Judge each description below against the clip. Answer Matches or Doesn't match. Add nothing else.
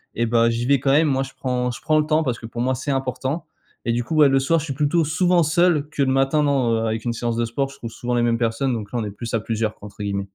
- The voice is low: Matches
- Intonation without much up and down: Doesn't match